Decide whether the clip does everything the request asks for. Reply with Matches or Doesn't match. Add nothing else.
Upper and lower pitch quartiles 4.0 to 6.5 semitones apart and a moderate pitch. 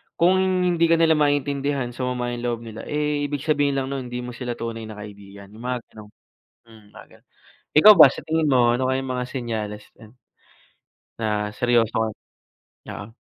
Doesn't match